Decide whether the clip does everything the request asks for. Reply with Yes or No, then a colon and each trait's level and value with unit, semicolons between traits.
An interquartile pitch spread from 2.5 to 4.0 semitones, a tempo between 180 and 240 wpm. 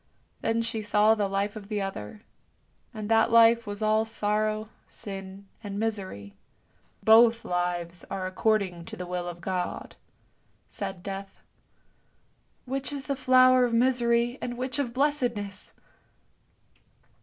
No: average, 3.3 semitones; average, 145 wpm